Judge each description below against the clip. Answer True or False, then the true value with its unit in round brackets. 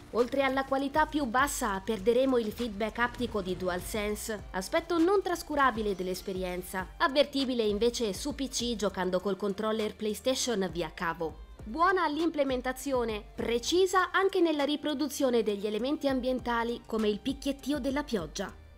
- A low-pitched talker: False (240 Hz)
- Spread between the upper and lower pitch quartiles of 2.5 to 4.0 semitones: False (4.9 semitones)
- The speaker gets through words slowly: False (125 wpm)